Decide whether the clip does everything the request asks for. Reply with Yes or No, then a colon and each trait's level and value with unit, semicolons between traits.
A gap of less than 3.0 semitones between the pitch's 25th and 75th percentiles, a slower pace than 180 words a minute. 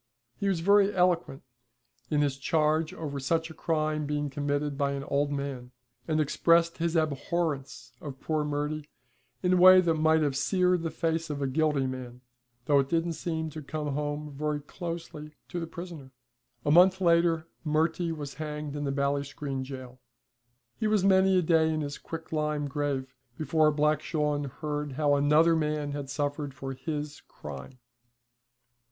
Yes: narrow, 2.4 semitones; average, 165 wpm